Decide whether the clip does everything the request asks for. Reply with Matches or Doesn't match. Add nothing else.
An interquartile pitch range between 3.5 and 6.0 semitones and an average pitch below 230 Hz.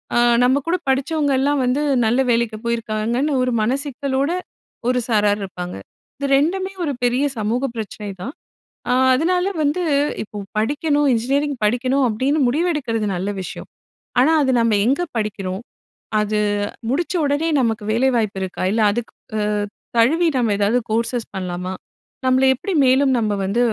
Doesn't match